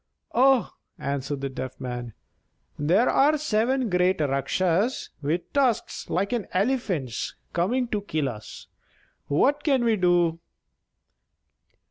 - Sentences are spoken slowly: Yes, slow, 115 wpm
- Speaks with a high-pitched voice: No, medium, 180 Hz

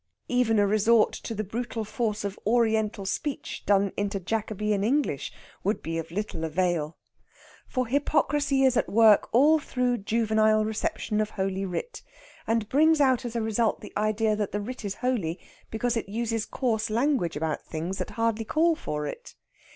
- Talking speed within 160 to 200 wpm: Yes, average, 170 wpm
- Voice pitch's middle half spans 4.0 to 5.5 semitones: No, average, 3.3 semitones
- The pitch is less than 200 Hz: No, high, 220 Hz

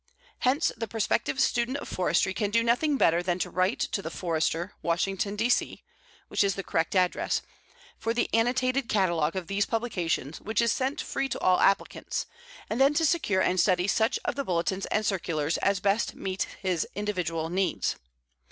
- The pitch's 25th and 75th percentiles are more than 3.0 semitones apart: Yes, average, 4.5 semitones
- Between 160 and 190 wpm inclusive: Yes, average, 180 wpm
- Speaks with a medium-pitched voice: No, high, 195 Hz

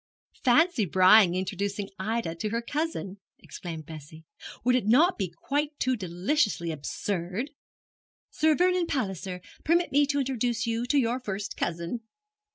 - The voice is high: Yes, high, 220 Hz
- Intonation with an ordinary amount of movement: No, wide, 6.9 semitones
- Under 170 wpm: Yes, average, 140 wpm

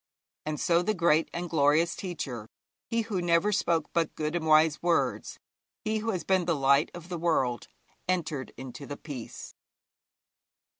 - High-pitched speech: No, medium, 165 Hz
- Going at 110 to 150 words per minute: No, average, 160 wpm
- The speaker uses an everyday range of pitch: Yes, average, 3.1 semitones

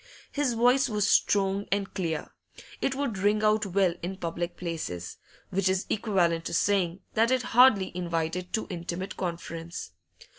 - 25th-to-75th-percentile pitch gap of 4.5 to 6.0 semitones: No, average, 3.7 semitones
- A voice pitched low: No, high, 190 Hz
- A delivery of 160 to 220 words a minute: No, average, 150 wpm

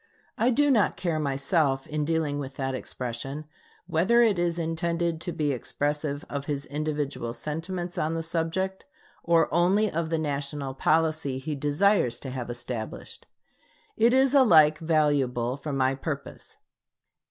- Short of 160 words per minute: Yes, average, 145 wpm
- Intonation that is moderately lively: Yes, average, 3.5 semitones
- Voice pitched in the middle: Yes, medium, 155 Hz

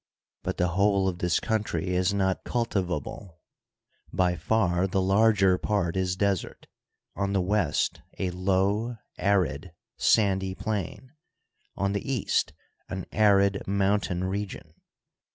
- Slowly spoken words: Yes, slow, 130 wpm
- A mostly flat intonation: Yes, narrow, 2.0 semitones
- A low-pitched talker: Yes, very low, 95 Hz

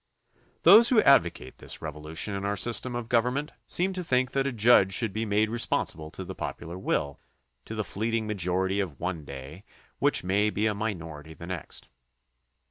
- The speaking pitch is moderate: No, low, 100 Hz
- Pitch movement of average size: No, wide, 5.7 semitones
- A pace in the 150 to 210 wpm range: Yes, average, 180 wpm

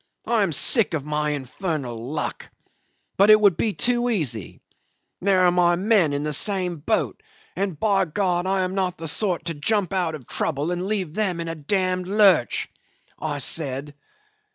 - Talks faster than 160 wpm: Yes, average, 180 wpm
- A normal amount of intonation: Yes, average, 4.7 semitones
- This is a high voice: No, medium, 180 Hz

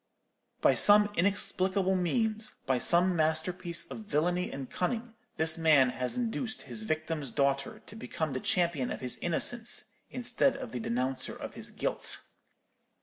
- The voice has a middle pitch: Yes, medium, 175 Hz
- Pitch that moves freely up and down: Yes, wide, 6.4 semitones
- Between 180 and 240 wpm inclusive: No, average, 145 wpm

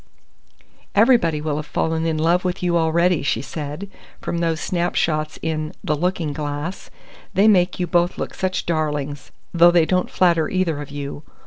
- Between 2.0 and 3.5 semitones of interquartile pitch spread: Yes, narrow, 2.6 semitones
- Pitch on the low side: No, medium, 165 Hz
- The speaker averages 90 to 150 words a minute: No, average, 165 wpm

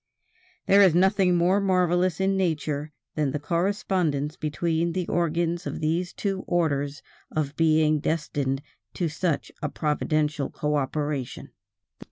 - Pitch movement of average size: Yes, average, 3.2 semitones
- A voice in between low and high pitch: Yes, medium, 160 Hz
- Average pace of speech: No, slow, 125 wpm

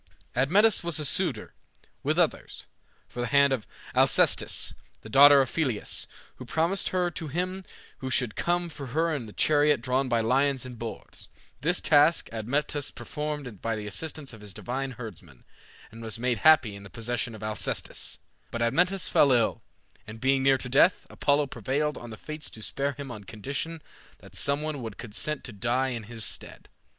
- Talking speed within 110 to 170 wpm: No, average, 180 wpm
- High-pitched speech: No, low, 135 Hz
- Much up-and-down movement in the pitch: No, average, 4.6 semitones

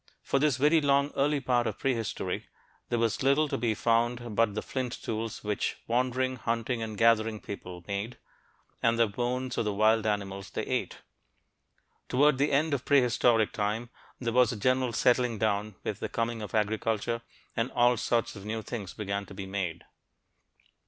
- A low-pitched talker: Yes, low, 115 Hz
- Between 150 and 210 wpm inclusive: Yes, average, 175 wpm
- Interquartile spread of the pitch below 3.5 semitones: Yes, average, 2.9 semitones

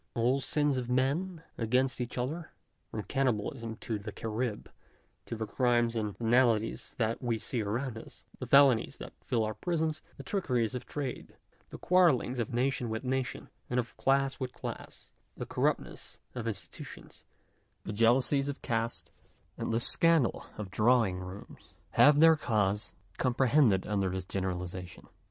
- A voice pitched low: Yes, low, 120 Hz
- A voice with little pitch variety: No, average, 3.6 semitones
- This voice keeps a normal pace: Yes, average, 155 wpm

